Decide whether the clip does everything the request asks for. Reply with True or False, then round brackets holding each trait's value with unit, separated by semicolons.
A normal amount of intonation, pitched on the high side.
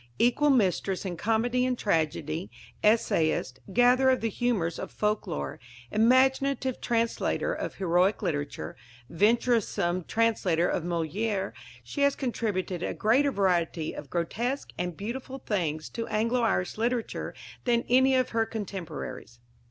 False (5.8 semitones; 215 Hz)